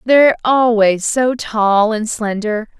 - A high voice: Yes, high, 225 Hz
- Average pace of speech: No, slow, 130 wpm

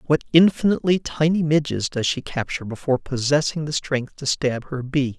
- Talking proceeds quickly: No, average, 175 wpm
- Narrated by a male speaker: Yes, male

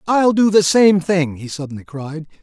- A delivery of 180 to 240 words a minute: Yes, average, 200 wpm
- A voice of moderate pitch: Yes, medium, 175 Hz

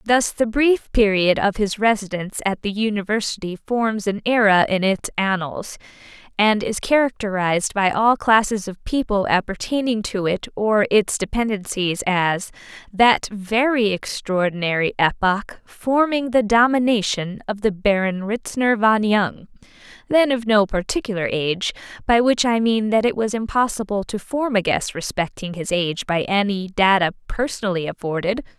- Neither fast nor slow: Yes, average, 145 wpm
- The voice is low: No, high, 210 Hz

